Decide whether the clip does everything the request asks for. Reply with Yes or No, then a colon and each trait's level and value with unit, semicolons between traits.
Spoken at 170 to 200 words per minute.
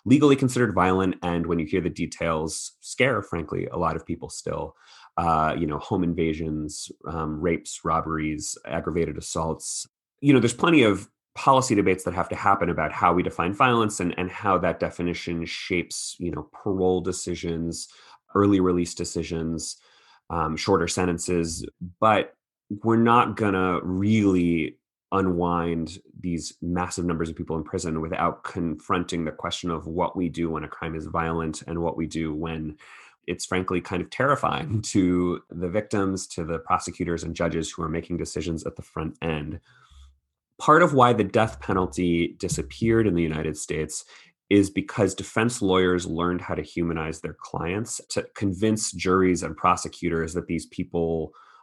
No: average, 160 wpm